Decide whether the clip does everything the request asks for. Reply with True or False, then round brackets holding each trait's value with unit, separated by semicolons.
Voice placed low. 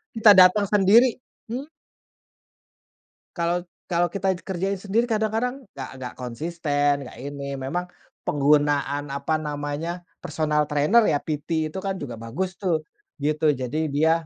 False (160 Hz)